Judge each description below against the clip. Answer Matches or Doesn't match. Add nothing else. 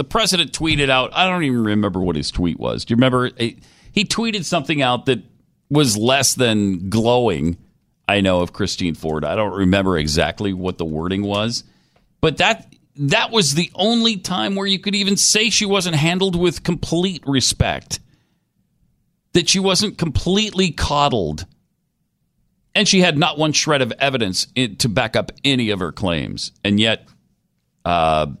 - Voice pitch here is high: Doesn't match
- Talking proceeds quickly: Doesn't match